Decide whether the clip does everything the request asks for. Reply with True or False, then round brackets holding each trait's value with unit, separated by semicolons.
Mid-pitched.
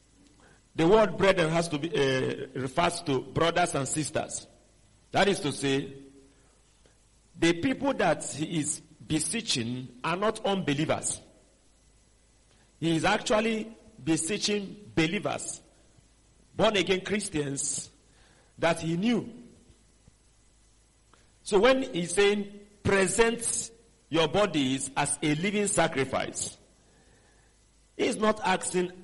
True (165 Hz)